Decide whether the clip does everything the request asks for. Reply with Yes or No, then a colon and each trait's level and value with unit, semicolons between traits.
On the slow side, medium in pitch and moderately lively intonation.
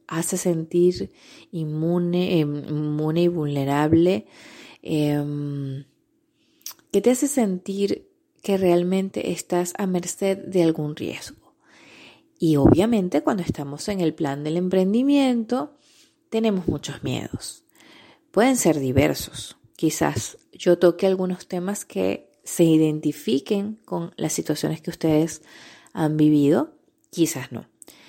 No: slow, 110 wpm; medium, 180 Hz; wide, 6.3 semitones